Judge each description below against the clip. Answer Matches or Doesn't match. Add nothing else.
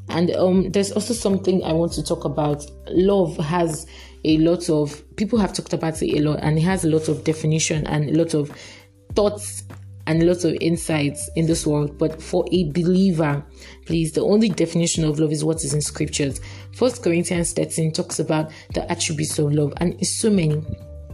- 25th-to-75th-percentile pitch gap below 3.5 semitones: Matches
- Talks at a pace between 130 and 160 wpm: Doesn't match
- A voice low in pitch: Doesn't match